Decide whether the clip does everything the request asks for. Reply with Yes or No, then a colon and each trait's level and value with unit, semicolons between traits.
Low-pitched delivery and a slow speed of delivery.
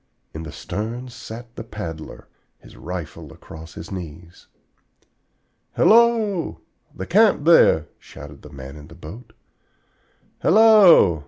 Yes: very low, 95 Hz; slow, 115 wpm